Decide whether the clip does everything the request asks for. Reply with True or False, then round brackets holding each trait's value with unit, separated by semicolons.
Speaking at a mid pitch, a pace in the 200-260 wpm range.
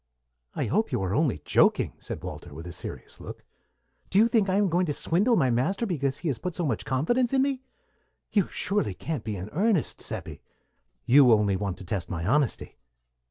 True (150 Hz; 205 wpm)